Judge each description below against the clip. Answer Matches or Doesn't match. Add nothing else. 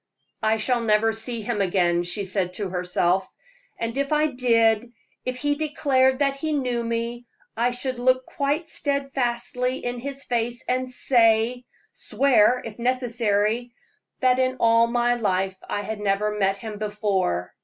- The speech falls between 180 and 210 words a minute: Doesn't match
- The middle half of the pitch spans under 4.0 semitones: Matches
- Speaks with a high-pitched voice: Matches